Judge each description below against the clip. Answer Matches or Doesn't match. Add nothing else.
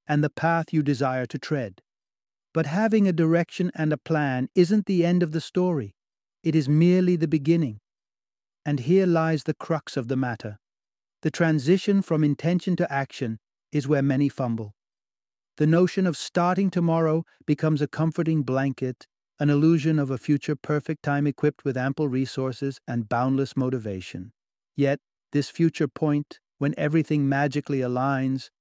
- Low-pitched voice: Doesn't match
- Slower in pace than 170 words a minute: Matches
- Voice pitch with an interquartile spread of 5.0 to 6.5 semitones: Doesn't match